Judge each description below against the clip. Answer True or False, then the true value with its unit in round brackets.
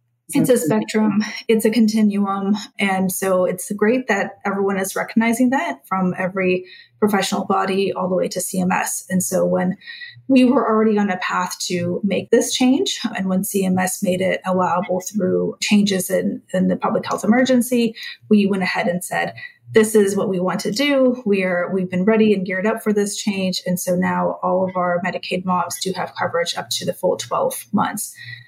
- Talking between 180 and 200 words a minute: True (190 wpm)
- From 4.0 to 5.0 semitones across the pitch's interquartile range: False (3.1 semitones)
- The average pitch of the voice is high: True (195 Hz)